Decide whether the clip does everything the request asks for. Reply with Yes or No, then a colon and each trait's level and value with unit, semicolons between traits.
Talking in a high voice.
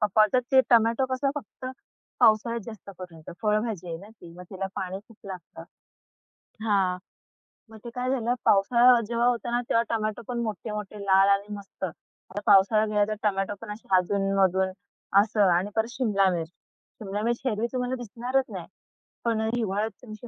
Yes: high, 215 Hz